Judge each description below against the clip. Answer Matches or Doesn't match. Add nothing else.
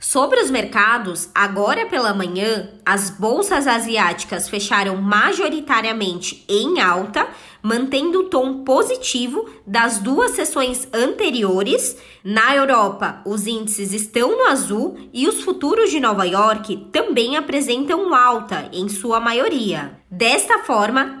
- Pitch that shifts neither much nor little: Doesn't match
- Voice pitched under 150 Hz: Doesn't match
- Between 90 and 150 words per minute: Matches